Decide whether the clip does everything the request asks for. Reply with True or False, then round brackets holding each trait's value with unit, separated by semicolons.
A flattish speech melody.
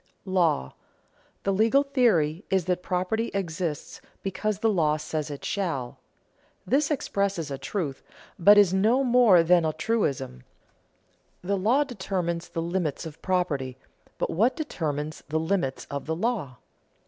False (4.8 semitones)